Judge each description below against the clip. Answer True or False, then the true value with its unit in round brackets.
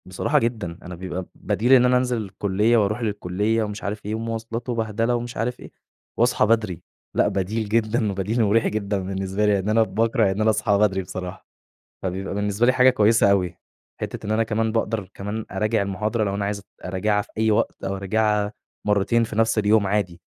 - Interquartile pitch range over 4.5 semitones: False (2.4 semitones)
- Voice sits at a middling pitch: False (105 Hz)